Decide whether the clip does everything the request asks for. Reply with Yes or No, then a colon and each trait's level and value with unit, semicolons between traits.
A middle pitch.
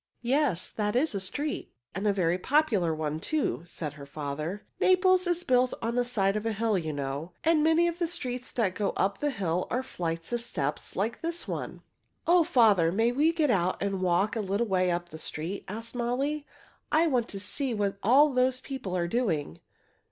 No: high, 215 Hz